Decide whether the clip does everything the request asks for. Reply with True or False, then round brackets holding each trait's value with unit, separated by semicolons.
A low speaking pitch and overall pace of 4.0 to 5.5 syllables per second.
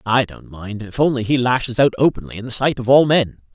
False (120 Hz; 5.9 syllables/s)